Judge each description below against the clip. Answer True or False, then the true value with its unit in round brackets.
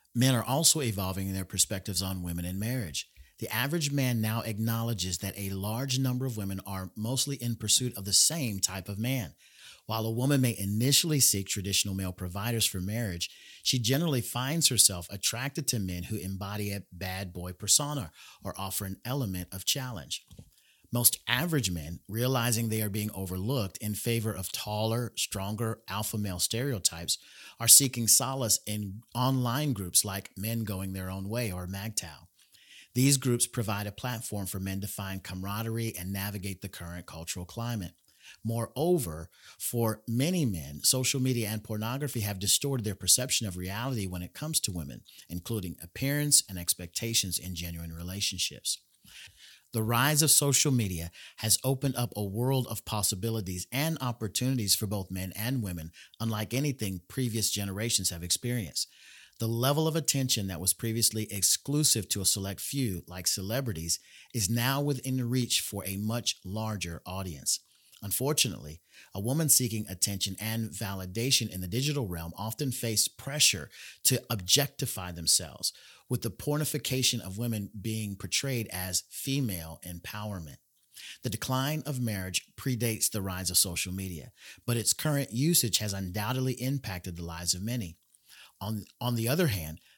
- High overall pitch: False (110 Hz)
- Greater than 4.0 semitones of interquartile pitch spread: True (4.7 semitones)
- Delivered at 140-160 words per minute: True (155 wpm)